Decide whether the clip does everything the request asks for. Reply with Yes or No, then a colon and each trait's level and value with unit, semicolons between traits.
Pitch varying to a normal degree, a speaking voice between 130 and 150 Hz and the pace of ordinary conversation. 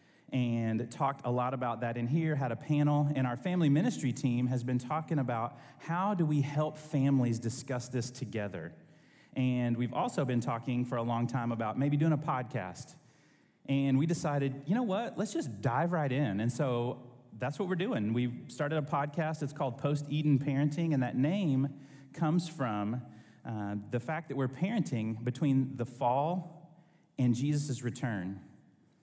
Yes: average, 3.7 semitones; low, 135 Hz; average, 175 wpm